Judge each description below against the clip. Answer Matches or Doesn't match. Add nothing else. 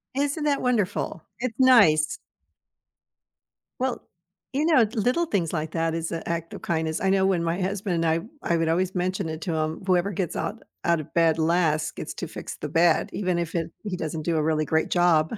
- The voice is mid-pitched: Matches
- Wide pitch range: Doesn't match